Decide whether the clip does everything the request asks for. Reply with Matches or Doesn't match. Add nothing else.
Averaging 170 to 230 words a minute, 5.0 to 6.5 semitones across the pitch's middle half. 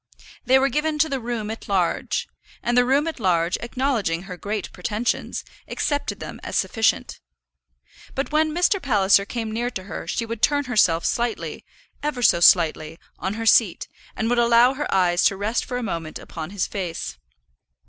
Matches